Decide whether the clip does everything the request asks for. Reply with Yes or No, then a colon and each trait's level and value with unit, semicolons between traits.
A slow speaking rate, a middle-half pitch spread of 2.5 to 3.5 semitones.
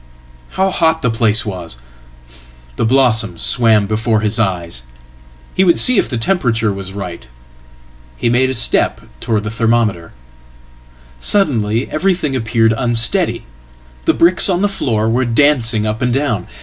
No: slow, 130 wpm; average, 3.9 semitones